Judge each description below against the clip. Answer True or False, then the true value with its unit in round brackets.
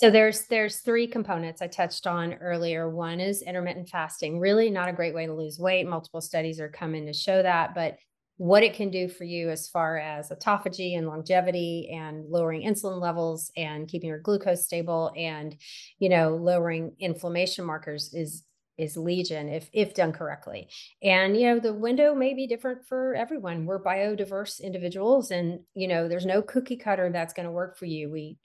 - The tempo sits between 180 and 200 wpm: True (190 wpm)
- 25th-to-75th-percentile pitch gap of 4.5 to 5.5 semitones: False (3.2 semitones)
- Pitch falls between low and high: True (175 Hz)